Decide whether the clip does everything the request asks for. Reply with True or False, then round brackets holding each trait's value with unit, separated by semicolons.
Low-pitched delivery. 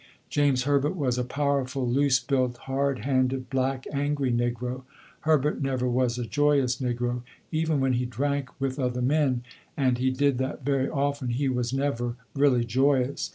True (130 Hz)